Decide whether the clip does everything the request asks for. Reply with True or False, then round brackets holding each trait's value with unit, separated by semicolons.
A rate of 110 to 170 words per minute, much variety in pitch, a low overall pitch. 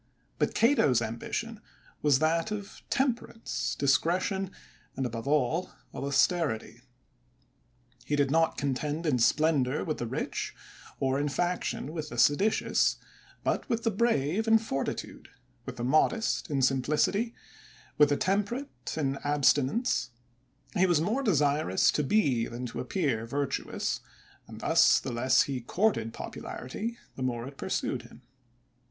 False (135 wpm; 6.7 semitones; 150 Hz)